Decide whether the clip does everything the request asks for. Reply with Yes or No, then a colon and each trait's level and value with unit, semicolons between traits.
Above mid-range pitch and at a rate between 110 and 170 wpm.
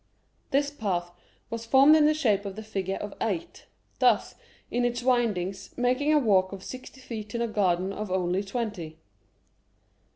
Yes: high, 215 Hz; average, 165 wpm